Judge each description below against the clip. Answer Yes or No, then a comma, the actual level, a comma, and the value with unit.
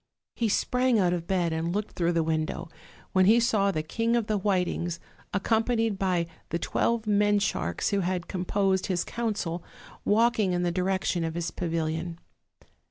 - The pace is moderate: Yes, average, 165 wpm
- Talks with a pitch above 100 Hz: Yes, high, 190 Hz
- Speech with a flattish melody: No, average, 3.7 semitones